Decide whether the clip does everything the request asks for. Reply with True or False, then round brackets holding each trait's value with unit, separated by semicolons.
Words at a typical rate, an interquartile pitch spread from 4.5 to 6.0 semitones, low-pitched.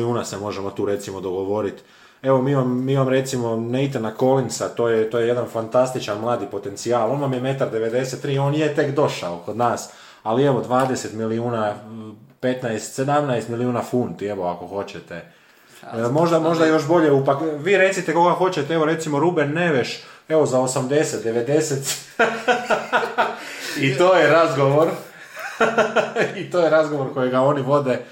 True (150 wpm; 4.8 semitones; 130 Hz)